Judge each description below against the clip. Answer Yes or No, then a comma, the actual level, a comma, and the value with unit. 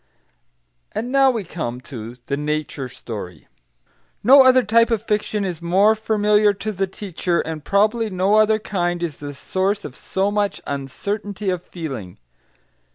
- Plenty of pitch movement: Yes, wide, 5.8 semitones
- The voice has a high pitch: Yes, high, 195 Hz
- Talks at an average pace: Yes, average, 155 wpm